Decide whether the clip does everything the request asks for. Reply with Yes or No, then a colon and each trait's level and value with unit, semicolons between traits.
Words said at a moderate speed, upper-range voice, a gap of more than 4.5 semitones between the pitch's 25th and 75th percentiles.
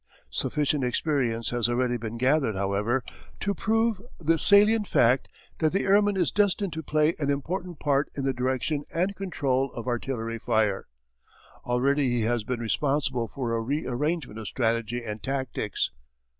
No: average, 155 wpm; low, 135 Hz; average, 5.2 semitones